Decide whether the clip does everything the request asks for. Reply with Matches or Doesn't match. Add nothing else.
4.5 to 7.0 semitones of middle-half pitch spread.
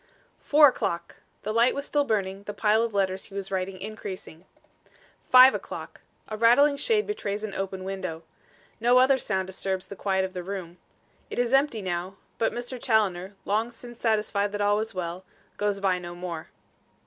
Doesn't match